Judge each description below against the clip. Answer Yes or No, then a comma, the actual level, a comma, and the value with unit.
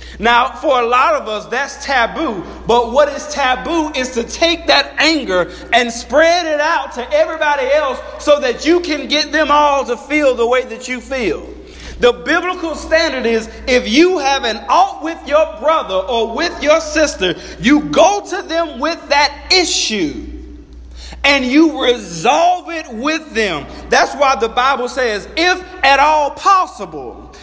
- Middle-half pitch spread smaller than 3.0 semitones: No, average, 4.3 semitones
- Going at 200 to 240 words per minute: No, average, 165 wpm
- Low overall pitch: No, very high, 290 Hz